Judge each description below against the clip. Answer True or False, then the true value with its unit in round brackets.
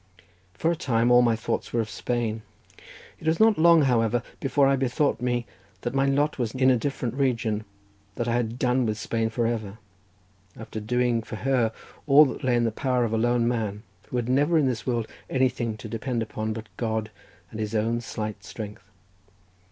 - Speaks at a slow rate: False (200 wpm)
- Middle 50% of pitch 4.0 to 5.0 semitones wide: False (2.7 semitones)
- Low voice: True (120 Hz)